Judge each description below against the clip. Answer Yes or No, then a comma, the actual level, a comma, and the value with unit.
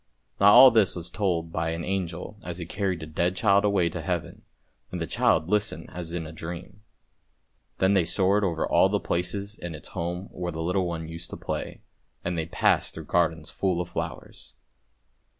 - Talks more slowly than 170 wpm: No, average, 195 wpm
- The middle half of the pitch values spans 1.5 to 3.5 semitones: Yes, average, 2.8 semitones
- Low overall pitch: Yes, very low, 90 Hz